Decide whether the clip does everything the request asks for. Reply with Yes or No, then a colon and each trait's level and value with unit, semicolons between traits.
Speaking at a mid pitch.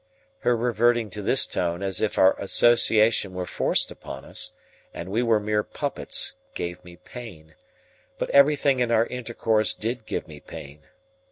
No: low, 110 Hz